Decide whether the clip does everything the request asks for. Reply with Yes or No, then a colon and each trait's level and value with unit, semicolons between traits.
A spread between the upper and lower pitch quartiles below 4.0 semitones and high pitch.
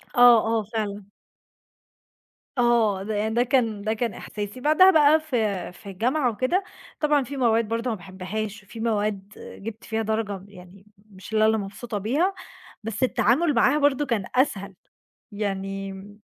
Yes: average, 3.4 semitones; high, 220 Hz